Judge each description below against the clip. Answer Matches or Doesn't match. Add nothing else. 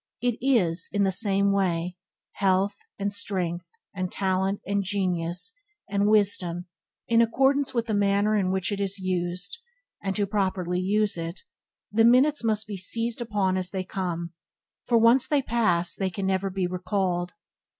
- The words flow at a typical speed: Matches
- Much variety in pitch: Doesn't match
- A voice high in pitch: Matches